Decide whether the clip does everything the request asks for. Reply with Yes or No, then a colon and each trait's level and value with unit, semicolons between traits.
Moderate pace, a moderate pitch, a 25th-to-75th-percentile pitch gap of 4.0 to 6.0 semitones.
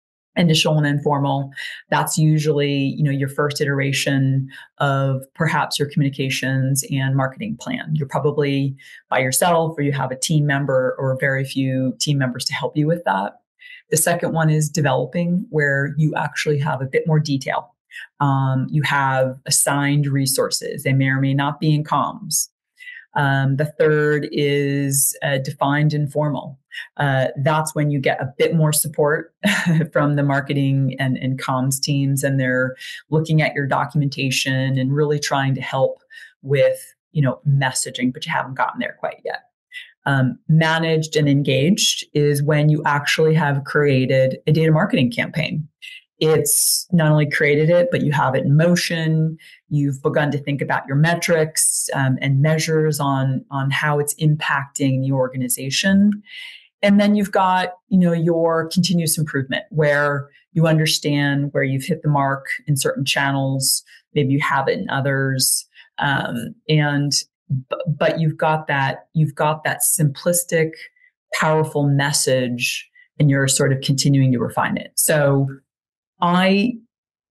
No: average, 155 wpm; medium, 145 Hz; average, 2.7 semitones